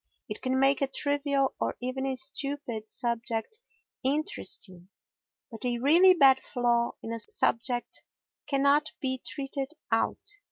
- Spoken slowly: Yes, slow, 130 wpm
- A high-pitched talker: Yes, very high, 265 Hz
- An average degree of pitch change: Yes, average, 3.0 semitones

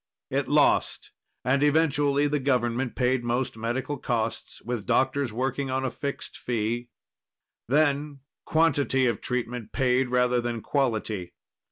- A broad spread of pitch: No, average, 2.7 semitones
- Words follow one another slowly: Yes, slow, 130 wpm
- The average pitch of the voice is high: No, low, 130 Hz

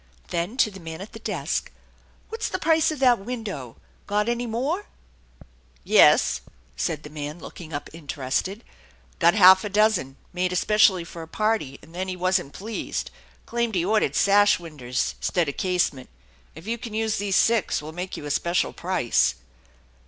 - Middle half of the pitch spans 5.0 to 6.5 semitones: Yes, wide, 5.5 semitones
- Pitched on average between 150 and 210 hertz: Yes, medium, 185 Hz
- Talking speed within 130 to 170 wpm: No, average, 185 wpm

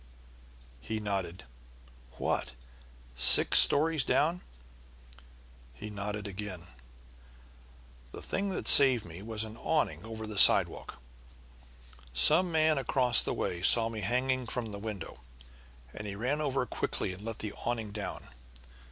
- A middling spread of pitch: Yes, average, 4.4 semitones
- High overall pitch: No, low, 110 Hz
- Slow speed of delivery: Yes, slow, 130 wpm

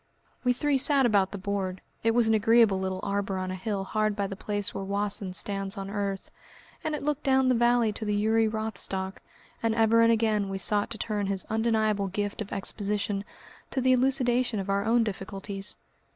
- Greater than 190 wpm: Yes, fast, 205 wpm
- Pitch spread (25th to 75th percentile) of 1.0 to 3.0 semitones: Yes, narrow, 2.6 semitones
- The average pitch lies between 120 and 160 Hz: No, high, 210 Hz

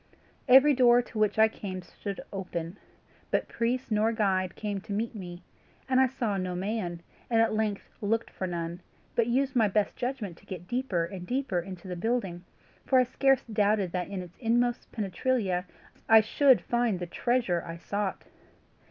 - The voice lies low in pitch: No, high, 210 Hz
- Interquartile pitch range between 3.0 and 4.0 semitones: No, average, 4.6 semitones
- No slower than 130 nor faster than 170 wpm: No, average, 180 wpm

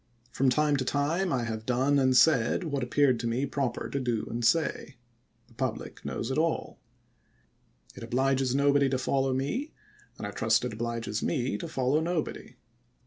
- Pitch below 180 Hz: Yes, low, 135 Hz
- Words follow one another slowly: No, average, 175 wpm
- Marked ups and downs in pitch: No, average, 2.9 semitones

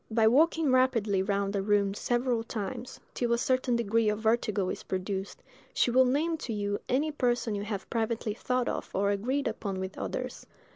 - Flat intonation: No, average, 3.9 semitones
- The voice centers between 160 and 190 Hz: No, high, 225 Hz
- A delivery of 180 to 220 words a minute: Yes, average, 185 wpm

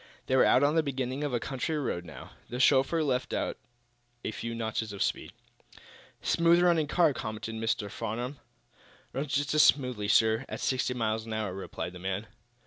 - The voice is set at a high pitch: No, low, 125 Hz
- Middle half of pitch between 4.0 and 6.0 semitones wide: Yes, average, 4.5 semitones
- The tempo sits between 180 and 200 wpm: Yes, average, 185 wpm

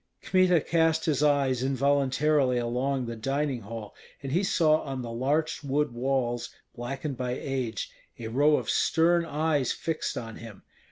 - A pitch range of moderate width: Yes, average, 4.0 semitones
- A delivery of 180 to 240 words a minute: No, average, 155 wpm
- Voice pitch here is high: No, low, 135 Hz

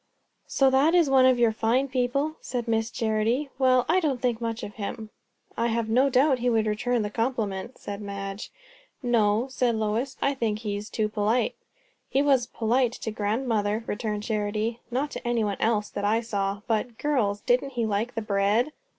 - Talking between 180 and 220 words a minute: Yes, average, 185 wpm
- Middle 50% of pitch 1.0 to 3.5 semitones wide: Yes, average, 3.1 semitones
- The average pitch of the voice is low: No, high, 230 Hz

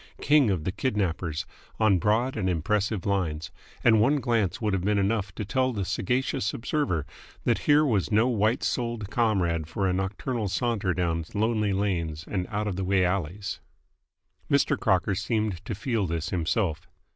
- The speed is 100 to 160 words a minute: No, average, 170 wpm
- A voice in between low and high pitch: No, low, 100 Hz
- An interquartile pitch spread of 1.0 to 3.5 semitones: No, average, 3.9 semitones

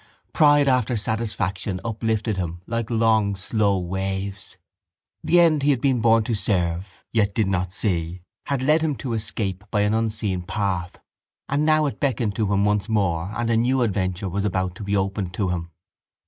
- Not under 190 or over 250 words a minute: No, average, 180 wpm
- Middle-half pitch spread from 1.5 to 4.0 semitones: Yes, average, 3.4 semitones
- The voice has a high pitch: No, low, 105 Hz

